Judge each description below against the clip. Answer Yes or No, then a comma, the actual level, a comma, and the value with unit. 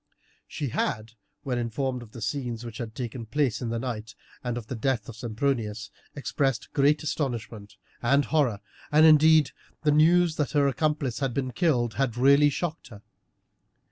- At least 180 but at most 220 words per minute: No, average, 170 wpm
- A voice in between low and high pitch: No, low, 130 Hz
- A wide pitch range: No, average, 4.2 semitones